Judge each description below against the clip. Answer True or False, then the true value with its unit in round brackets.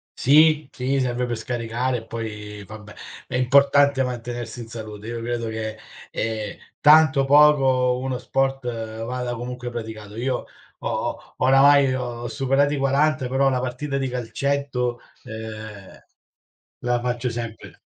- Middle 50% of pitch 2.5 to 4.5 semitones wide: True (2.8 semitones)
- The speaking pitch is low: True (125 Hz)